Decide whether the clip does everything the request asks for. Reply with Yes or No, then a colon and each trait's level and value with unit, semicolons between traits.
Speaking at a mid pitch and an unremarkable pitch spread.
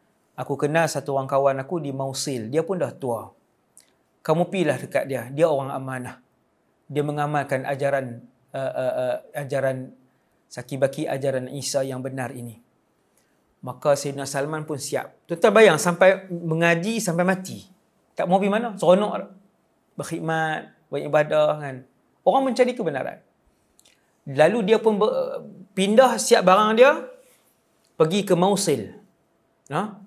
No: medium, 155 Hz; wide, 6.0 semitones